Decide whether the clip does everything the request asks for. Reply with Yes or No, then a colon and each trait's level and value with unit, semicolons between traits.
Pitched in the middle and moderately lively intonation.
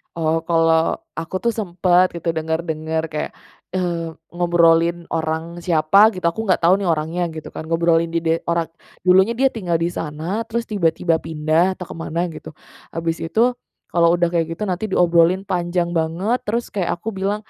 No: medium, 170 Hz; narrow, 2.1 semitones